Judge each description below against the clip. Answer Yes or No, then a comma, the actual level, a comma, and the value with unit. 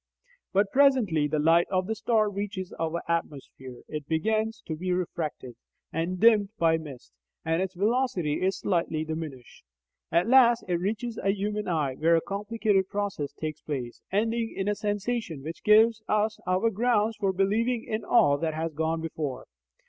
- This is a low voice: No, high, 190 Hz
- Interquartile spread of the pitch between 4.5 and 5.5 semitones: Yes, average, 5.2 semitones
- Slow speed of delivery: No, average, 165 wpm